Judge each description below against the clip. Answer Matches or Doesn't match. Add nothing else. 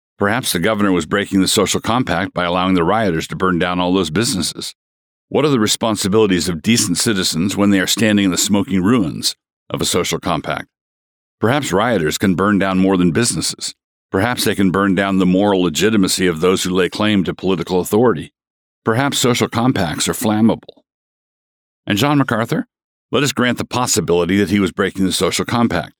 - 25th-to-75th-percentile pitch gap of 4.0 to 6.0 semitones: Doesn't match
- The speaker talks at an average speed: Matches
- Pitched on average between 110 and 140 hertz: Doesn't match